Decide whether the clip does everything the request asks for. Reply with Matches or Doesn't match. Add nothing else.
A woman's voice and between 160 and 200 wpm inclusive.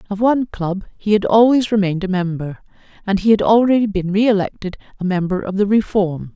Matches